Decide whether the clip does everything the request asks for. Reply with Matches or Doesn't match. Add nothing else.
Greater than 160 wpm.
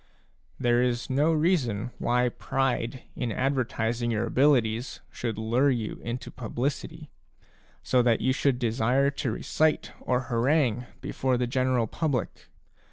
Doesn't match